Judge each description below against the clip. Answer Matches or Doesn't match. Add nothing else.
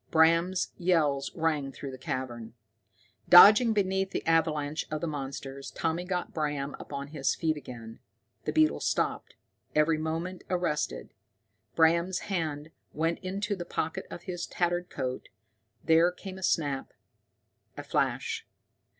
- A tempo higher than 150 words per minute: Doesn't match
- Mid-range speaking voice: Matches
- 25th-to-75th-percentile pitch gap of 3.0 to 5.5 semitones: Matches